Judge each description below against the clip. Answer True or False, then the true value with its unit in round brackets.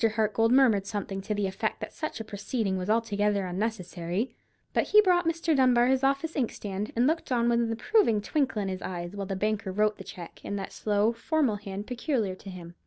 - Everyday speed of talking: False (210 wpm)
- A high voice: True (215 Hz)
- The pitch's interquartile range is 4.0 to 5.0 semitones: True (4.3 semitones)